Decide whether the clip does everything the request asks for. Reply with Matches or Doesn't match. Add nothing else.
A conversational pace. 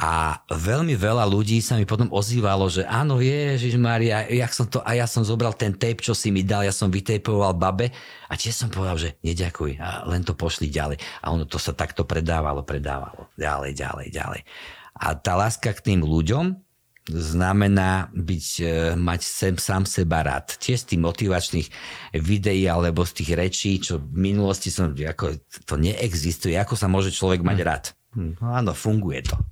Doesn't match